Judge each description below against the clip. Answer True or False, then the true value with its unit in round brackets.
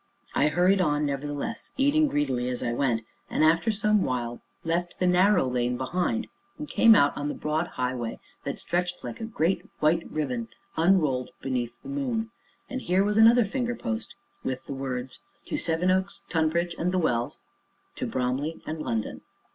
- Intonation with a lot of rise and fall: True (7.1 semitones)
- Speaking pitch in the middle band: True (165 Hz)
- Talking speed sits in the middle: True (170 wpm)